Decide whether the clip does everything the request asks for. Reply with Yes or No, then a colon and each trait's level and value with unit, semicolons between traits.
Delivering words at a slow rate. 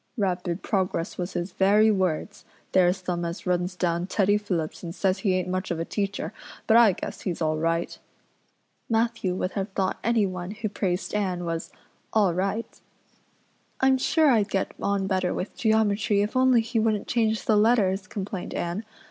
No: average, 175 wpm